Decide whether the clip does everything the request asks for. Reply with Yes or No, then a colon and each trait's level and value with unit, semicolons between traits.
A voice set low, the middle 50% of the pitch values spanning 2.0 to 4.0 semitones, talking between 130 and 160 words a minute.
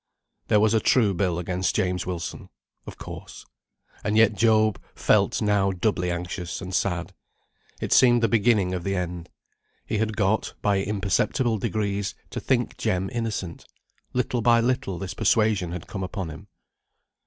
Yes: low, 100 Hz; average, 3.2 semitones; average, 155 wpm